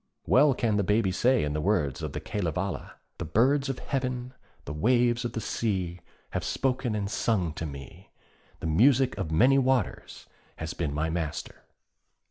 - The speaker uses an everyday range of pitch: No, wide, 7.6 semitones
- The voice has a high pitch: No, low, 105 Hz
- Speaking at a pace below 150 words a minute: No, average, 170 wpm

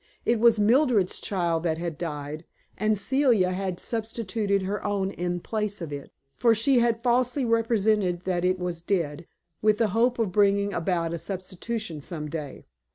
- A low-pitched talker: No, high, 200 Hz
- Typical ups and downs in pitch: Yes, average, 4.5 semitones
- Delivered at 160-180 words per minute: Yes, average, 165 wpm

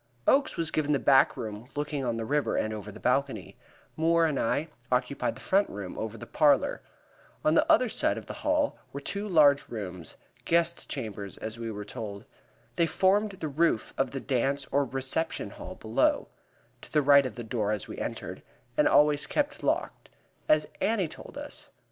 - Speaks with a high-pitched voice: No, medium, 140 Hz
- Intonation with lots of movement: Yes, wide, 6.1 semitones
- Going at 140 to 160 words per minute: No, average, 185 wpm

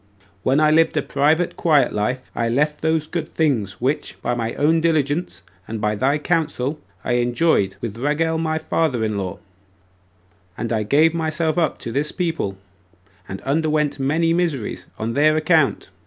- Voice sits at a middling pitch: Yes, medium, 150 Hz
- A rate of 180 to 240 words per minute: No, average, 165 wpm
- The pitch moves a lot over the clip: No, average, 5.0 semitones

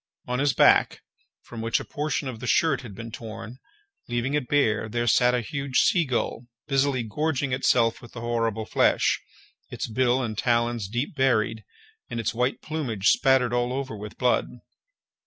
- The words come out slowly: No, average, 175 wpm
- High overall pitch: No, low, 120 Hz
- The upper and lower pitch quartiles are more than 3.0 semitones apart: No, average, 2.7 semitones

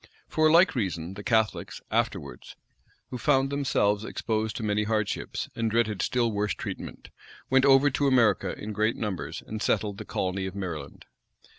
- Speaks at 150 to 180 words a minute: Yes, average, 170 wpm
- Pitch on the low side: Yes, low, 110 Hz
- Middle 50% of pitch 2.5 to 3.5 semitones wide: No, average, 4.0 semitones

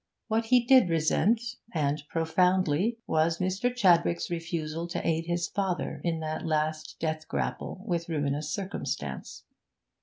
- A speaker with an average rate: No, slow, 130 wpm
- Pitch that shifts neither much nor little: Yes, average, 3.1 semitones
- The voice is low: No, medium, 170 Hz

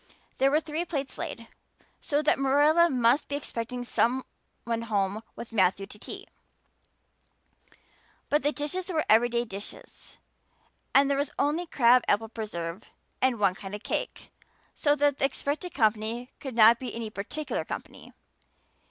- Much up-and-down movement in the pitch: No, average, 4.8 semitones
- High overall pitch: Yes, high, 245 Hz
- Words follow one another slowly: No, average, 150 wpm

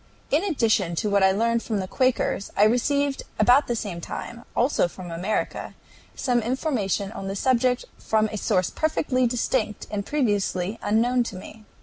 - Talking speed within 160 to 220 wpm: Yes, average, 165 wpm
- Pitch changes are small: No, average, 4.2 semitones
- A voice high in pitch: Yes, high, 225 Hz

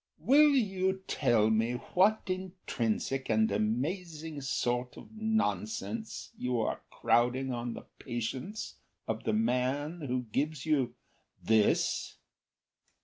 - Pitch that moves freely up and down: Yes, wide, 7.8 semitones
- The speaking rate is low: Yes, slow, 110 wpm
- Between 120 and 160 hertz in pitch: Yes, medium, 140 Hz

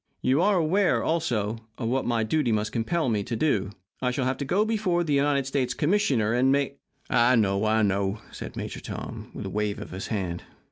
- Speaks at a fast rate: Yes, fast, 220 wpm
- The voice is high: No, low, 125 Hz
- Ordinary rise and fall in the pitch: No, wide, 5.8 semitones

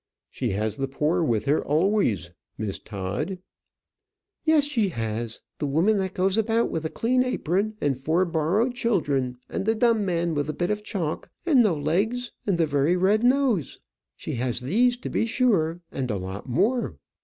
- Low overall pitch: No, medium, 175 Hz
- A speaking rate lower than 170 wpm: No, average, 180 wpm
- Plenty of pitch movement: Yes, wide, 8.1 semitones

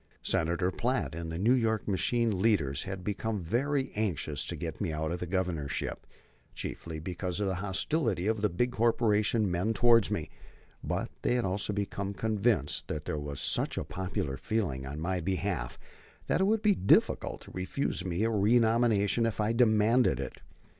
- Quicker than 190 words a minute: No, average, 175 wpm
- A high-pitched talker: No, low, 100 Hz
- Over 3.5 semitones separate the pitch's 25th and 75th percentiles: Yes, average, 4.6 semitones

